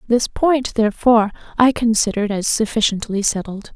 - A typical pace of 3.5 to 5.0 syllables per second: No, 5.4 syllables/s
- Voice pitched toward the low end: No, high, 220 Hz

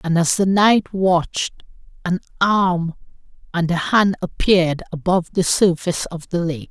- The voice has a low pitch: No, medium, 175 Hz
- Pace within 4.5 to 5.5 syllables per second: Yes, 4.6 syllables/s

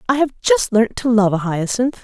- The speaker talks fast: Yes, fast, 235 wpm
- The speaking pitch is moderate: No, high, 235 Hz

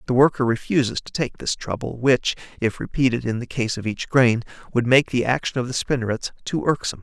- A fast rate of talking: Yes, fast, 215 wpm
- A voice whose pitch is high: No, low, 125 Hz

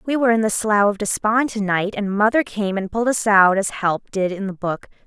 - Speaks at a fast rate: Yes, fast, 250 wpm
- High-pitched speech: Yes, high, 210 Hz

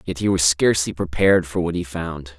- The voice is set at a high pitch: No, very low, 85 Hz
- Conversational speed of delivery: No, fast, 225 wpm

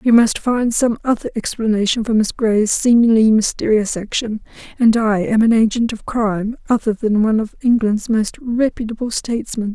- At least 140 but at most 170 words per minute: Yes, average, 160 wpm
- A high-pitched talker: Yes, high, 225 Hz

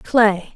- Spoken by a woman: Yes, female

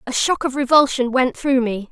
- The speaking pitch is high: Yes, very high, 260 Hz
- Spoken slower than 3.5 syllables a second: No, 5.1 syllables/s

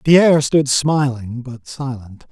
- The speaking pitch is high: No, low, 135 Hz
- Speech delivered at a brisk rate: No, slow, 130 wpm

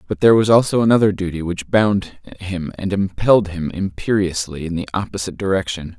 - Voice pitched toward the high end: No, very low, 95 Hz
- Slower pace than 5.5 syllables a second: No, 5.7 syllables/s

